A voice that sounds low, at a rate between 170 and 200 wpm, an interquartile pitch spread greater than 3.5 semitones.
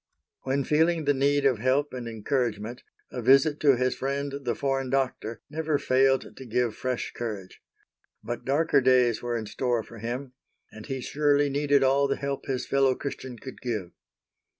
No: low, 130 Hz; average, 175 wpm; narrow, 2.6 semitones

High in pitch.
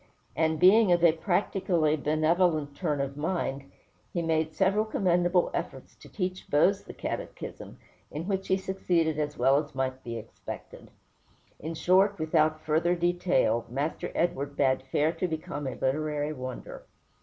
No: medium, 160 Hz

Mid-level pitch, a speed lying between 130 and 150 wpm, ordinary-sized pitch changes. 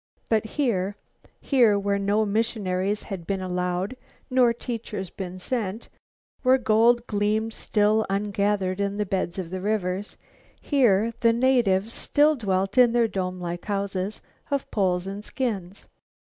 No: high, 205 Hz; average, 140 wpm; average, 3.3 semitones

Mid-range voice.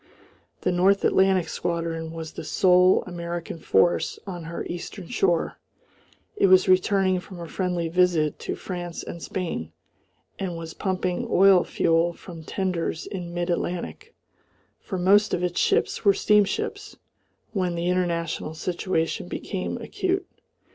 Yes: medium, 180 Hz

